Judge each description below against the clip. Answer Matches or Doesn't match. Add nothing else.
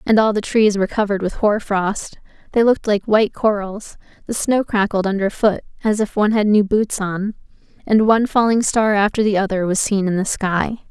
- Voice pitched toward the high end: Matches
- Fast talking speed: Matches